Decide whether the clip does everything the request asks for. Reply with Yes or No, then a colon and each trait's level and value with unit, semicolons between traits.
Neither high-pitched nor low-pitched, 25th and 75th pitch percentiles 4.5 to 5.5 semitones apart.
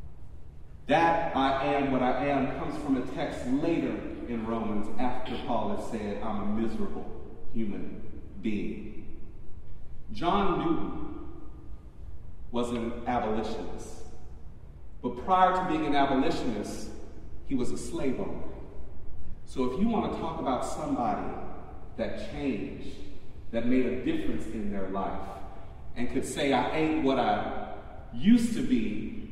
No: low, 115 Hz; average, 5.2 semitones